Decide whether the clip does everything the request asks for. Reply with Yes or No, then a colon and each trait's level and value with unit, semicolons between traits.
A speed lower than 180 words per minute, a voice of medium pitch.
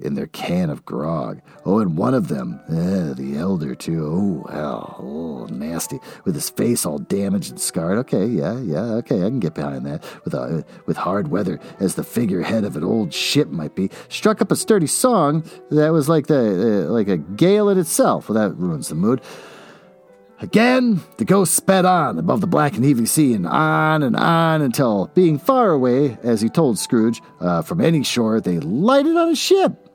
No: average, 200 wpm; medium, 155 Hz